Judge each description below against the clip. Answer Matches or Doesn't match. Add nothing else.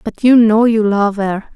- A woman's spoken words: Matches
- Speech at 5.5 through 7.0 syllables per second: Doesn't match